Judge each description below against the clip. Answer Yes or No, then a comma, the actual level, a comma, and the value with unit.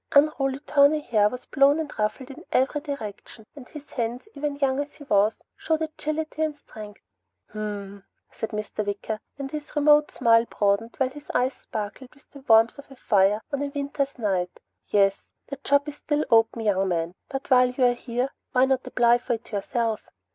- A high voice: Yes, very high, 255 Hz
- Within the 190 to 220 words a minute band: Yes, average, 195 wpm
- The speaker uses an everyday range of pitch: Yes, average, 4.9 semitones